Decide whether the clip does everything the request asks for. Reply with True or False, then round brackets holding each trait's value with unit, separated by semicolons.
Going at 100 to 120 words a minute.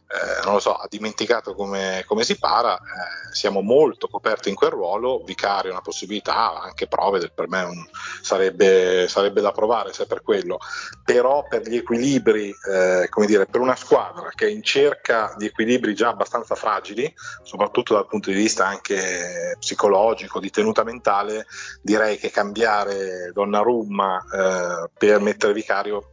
False (170 wpm)